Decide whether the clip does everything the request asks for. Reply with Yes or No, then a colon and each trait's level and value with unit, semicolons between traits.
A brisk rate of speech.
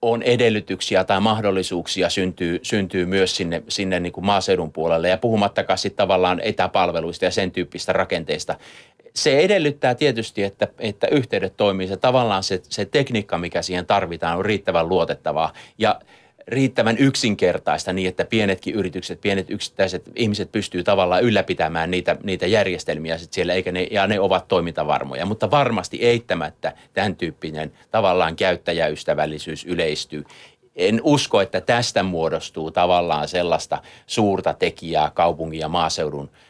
No: average, 140 wpm